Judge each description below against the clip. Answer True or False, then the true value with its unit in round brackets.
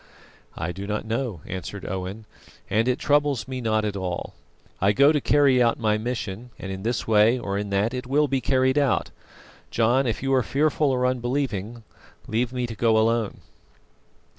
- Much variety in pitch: False (3.8 semitones)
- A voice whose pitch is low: True (115 Hz)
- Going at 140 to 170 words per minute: False (185 wpm)